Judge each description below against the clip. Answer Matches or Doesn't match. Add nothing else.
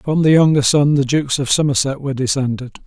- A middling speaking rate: Doesn't match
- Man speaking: Matches